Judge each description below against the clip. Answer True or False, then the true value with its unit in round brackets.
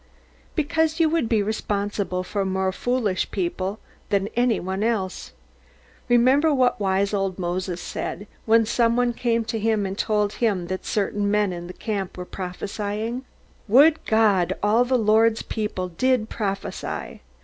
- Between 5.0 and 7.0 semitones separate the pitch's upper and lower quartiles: False (3.5 semitones)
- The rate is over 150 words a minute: False (145 wpm)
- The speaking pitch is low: False (210 Hz)